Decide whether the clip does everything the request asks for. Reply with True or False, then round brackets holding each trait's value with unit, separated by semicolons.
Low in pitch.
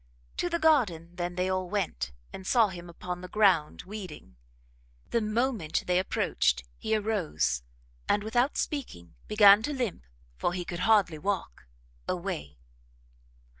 False (185 Hz)